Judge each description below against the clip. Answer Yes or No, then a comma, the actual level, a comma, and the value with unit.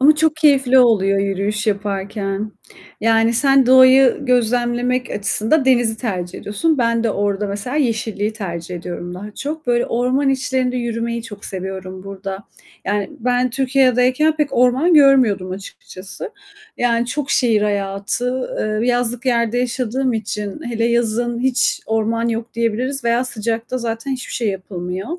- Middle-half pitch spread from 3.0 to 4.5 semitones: Yes, average, 3.6 semitones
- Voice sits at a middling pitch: No, high, 235 Hz